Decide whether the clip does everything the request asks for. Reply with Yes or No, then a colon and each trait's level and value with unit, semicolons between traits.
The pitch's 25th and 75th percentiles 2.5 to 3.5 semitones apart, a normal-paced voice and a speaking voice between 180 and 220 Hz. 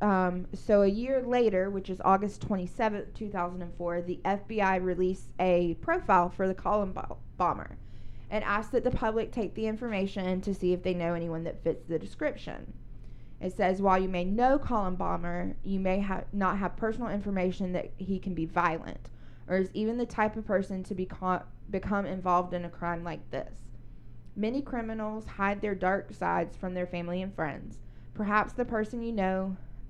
Yes: average, 3.0 semitones; average, 180 wpm; high, 190 Hz